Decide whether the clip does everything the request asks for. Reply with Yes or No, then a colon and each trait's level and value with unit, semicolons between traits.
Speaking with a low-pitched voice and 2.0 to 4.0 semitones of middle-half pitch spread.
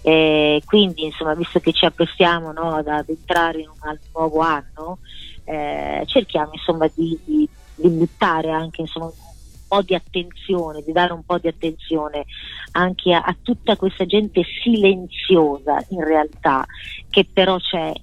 No: medium, 165 Hz; narrow, 2.6 semitones